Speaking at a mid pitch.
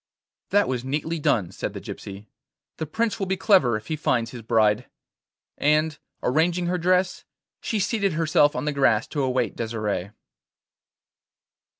Yes: medium, 145 Hz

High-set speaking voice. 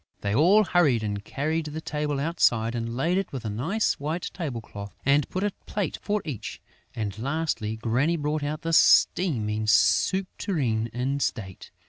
No: medium, 140 Hz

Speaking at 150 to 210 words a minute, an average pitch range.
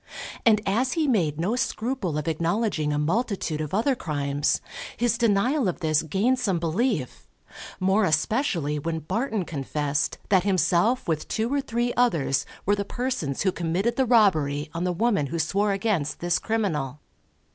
No: average, 160 wpm; wide, 6.8 semitones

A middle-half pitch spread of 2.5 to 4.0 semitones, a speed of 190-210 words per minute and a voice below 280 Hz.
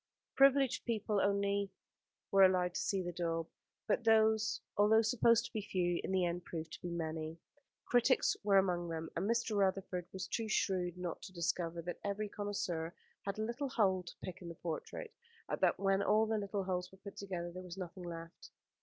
Yes: average, 3.2 semitones; average, 200 wpm; high, 190 Hz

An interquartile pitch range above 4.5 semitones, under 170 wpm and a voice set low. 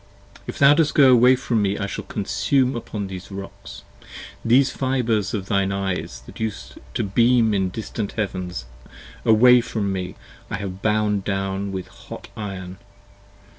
No: average, 3.4 semitones; average, 160 wpm; low, 105 Hz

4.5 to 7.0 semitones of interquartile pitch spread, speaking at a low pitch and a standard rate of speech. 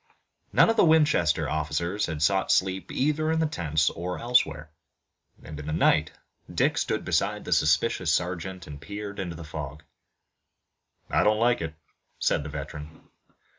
Yes: average, 5.2 semitones; very low, 85 Hz; average, 160 wpm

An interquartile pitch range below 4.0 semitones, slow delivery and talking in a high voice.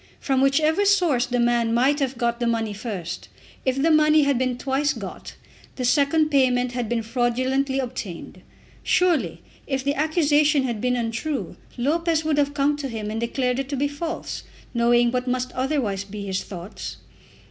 No: average, 3.4 semitones; average, 175 wpm; very high, 260 Hz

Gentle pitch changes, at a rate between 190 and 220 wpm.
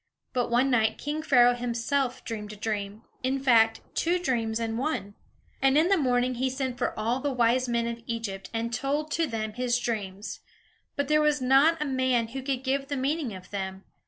No: average, 3.2 semitones; average, 200 wpm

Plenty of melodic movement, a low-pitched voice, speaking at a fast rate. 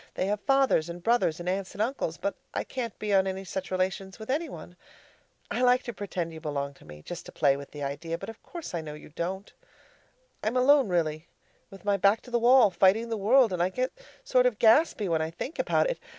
No: wide, 6.1 semitones; high, 195 Hz; fast, 240 wpm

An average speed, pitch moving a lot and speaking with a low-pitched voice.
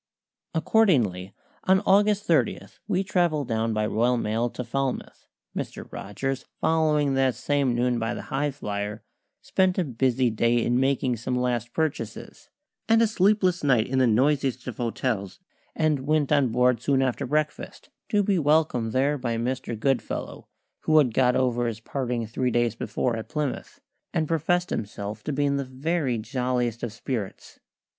No: average, 160 wpm; average, 4.3 semitones; low, 130 Hz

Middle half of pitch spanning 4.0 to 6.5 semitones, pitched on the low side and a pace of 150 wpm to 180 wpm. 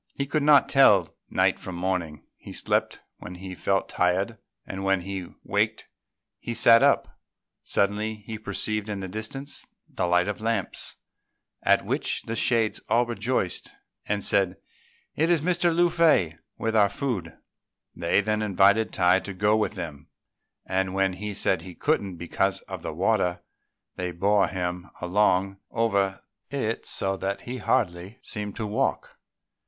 No: average, 3.5 semitones; low, 100 Hz; average, 155 wpm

